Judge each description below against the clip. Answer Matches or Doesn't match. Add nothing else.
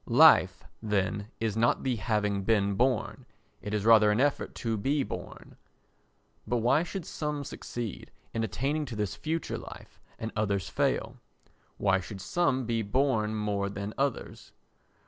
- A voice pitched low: Matches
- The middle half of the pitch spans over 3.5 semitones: Matches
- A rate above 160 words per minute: Doesn't match